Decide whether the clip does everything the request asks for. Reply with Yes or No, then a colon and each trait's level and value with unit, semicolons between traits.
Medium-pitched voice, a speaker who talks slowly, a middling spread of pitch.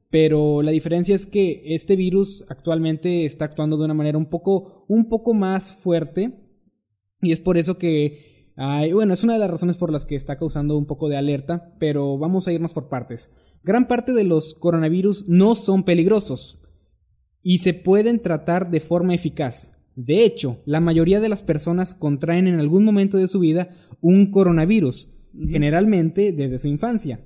No: medium, 170 Hz; average, 180 wpm; average, 4.2 semitones